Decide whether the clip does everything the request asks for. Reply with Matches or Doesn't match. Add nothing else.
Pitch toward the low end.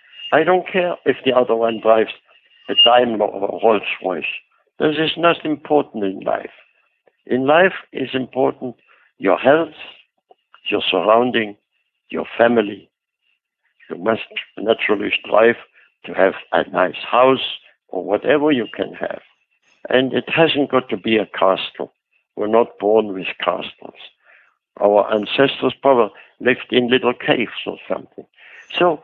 Matches